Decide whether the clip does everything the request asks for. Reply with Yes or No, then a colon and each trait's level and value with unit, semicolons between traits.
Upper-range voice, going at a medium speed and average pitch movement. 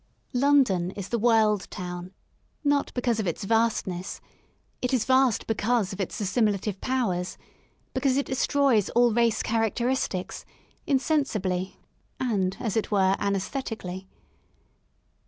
No: high, 220 Hz; slow, 120 wpm; average, 4.7 semitones